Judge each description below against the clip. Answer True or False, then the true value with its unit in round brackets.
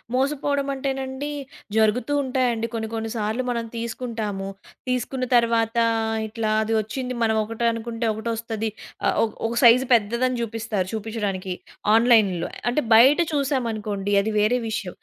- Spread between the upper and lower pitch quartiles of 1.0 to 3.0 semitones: True (2.6 semitones)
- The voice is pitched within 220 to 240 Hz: True (230 Hz)